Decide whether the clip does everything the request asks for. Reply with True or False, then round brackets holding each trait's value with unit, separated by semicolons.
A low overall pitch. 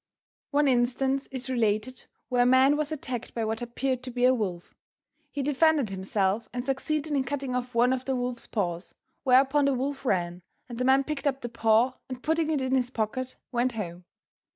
False (255 Hz)